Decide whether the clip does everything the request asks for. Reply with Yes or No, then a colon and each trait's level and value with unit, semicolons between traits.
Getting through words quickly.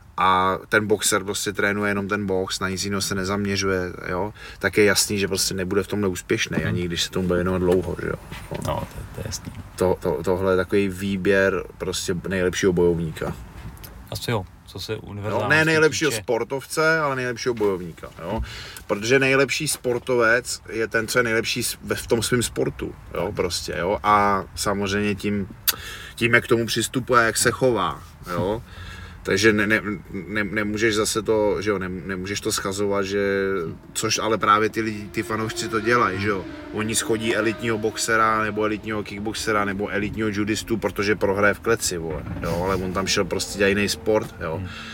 Yes: fast, 175 wpm